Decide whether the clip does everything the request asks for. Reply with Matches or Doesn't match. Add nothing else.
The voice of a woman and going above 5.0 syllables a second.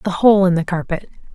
Matches